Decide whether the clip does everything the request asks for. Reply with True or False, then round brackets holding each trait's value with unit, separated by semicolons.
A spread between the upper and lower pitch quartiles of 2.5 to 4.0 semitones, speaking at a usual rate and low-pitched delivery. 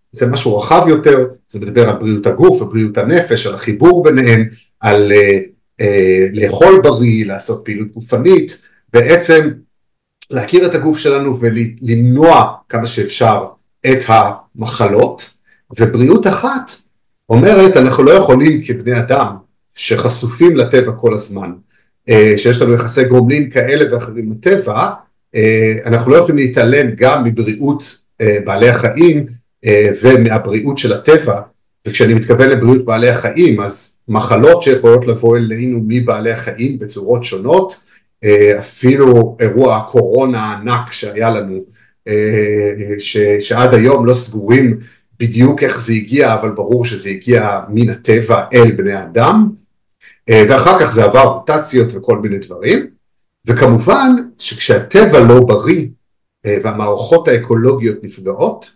True (3.7 semitones; 120 wpm; 120 Hz)